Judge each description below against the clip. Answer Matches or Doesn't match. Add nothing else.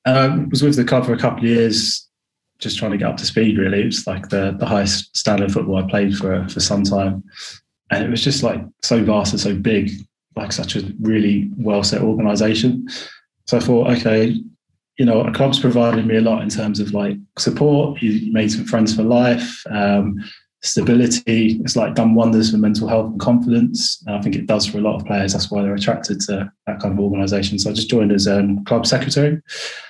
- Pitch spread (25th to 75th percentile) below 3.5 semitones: Matches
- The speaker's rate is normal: Doesn't match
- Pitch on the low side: Matches